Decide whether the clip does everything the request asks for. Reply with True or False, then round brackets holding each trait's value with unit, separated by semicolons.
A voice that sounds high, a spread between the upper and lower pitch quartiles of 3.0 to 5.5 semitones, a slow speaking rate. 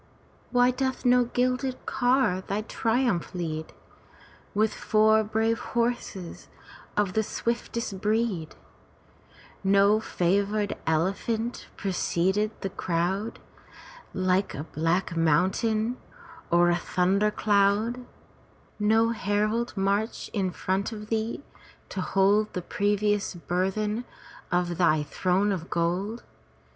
True (205 Hz; 3.4 semitones; 105 wpm)